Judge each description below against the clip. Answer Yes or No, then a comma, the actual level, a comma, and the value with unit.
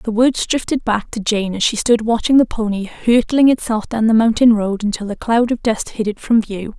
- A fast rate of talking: Yes, fast, 240 wpm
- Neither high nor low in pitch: No, high, 220 Hz